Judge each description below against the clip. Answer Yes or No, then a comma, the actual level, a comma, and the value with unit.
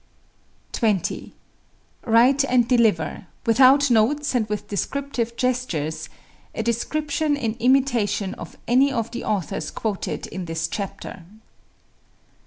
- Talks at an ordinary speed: No, slow, 110 wpm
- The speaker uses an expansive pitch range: No, average, 4.4 semitones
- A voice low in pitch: No, high, 235 Hz